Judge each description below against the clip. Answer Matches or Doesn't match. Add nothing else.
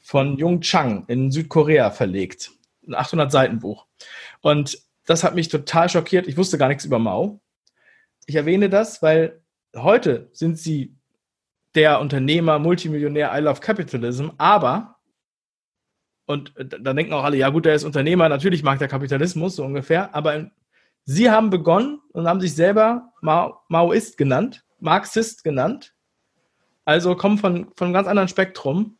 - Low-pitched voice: Doesn't match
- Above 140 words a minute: Matches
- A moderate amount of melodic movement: Matches